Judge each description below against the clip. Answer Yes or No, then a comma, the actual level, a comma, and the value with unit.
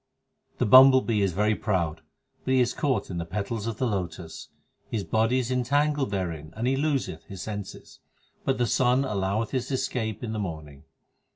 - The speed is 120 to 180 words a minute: No, average, 190 wpm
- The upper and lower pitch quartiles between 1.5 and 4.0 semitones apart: No, average, 5.2 semitones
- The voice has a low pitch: Yes, low, 110 Hz